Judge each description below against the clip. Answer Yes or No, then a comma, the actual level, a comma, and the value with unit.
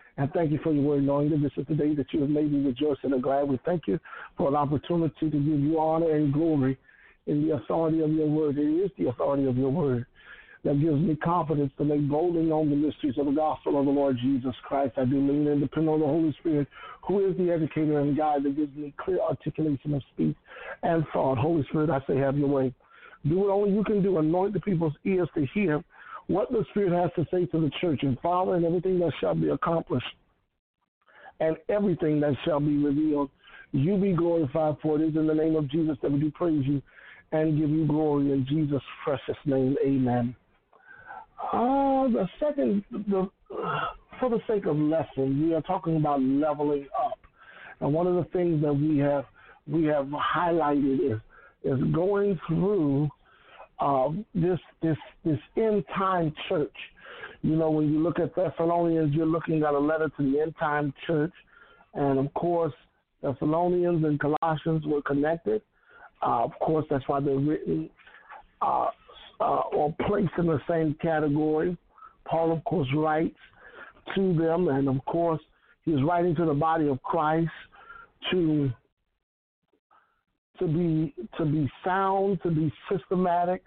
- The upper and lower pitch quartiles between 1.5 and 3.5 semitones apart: Yes, average, 3.2 semitones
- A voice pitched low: No, medium, 155 Hz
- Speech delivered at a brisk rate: No, average, 185 wpm